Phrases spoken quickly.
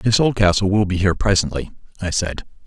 No: average, 180 wpm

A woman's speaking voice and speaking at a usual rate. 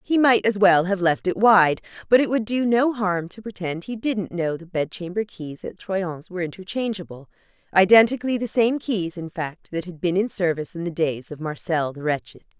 No: female; fast, 210 wpm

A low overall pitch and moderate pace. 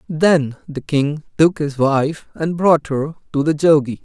No: medium, 150 Hz; average, 180 wpm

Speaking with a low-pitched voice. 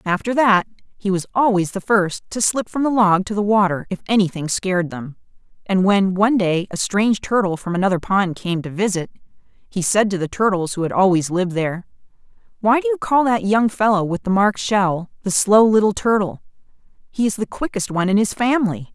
No: high, 200 Hz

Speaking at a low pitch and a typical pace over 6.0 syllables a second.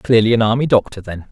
Yes: low, 110 Hz; 6.4 syllables/s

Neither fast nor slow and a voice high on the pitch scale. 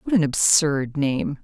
No: average, 165 wpm; medium, 155 Hz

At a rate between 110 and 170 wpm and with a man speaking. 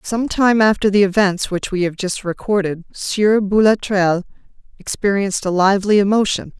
No: average, 145 wpm; female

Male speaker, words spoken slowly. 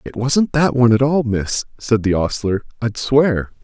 No: male; average, 200 wpm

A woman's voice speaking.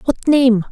Yes: female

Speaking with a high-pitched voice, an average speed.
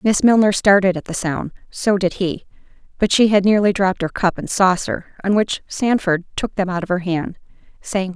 Yes: high, 195 Hz; average, 190 wpm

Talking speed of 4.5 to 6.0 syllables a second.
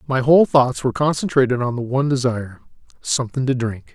No: 6.5 syllables/s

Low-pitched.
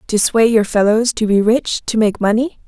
No: high, 220 Hz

